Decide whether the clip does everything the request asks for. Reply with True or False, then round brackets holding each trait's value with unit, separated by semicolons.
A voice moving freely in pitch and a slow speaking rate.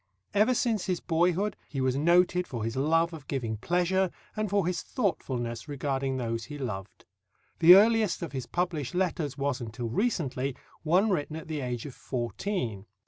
False (6.0 semitones; 170 wpm)